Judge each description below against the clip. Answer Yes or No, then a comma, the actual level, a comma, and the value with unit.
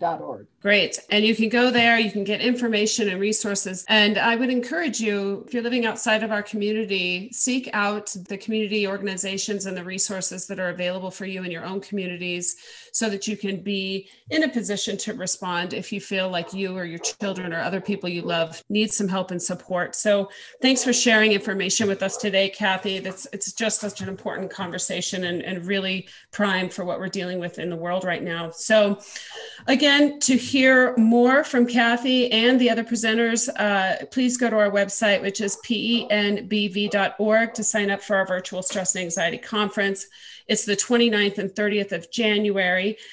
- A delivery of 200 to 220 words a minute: No, average, 190 wpm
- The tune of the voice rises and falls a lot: No, average, 2.7 semitones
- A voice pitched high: Yes, high, 205 Hz